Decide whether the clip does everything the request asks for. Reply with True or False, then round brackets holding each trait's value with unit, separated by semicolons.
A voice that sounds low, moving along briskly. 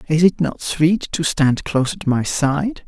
False (155 Hz; 210 wpm)